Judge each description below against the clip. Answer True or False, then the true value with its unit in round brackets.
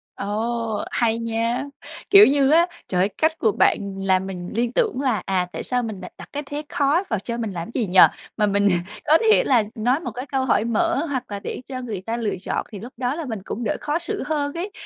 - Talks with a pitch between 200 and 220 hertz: False (235 Hz)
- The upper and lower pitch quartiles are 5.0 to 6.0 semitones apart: True (5.4 semitones)